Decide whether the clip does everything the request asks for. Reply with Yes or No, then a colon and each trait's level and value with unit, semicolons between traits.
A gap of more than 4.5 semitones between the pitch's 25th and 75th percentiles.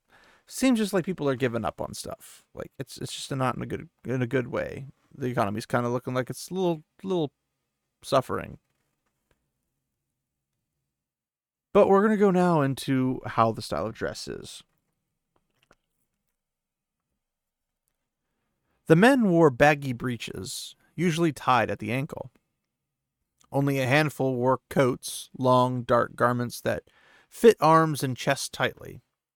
Yes: average, 5.1 semitones